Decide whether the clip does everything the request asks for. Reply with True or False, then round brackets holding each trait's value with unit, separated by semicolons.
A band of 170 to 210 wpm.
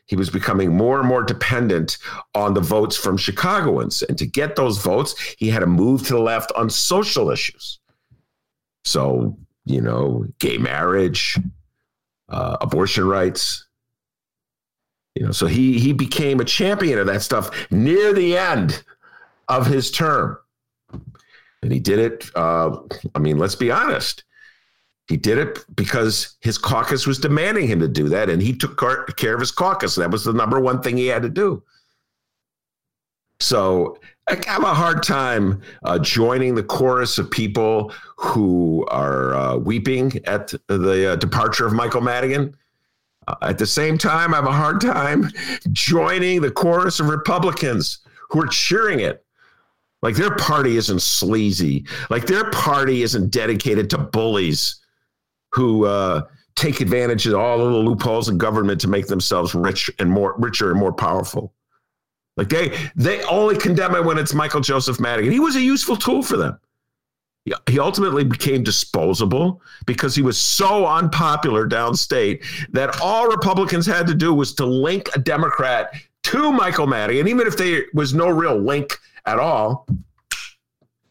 False (160 wpm)